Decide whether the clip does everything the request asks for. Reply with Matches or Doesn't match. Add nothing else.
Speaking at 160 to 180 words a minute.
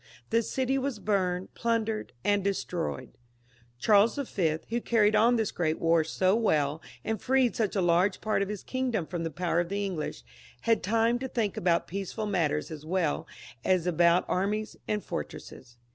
Matches